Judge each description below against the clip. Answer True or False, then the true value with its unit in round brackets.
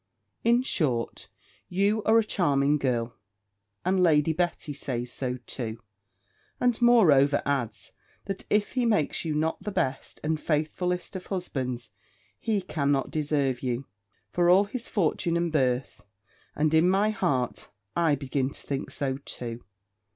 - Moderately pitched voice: True (155 Hz)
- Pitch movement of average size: False (5.7 semitones)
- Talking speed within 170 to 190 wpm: False (145 wpm)